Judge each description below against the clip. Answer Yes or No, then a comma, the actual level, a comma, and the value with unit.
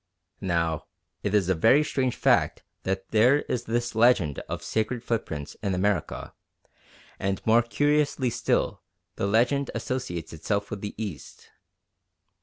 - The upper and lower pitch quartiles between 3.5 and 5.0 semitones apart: Yes, average, 4.4 semitones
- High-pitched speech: No, low, 110 Hz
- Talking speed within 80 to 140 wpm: Yes, slow, 135 wpm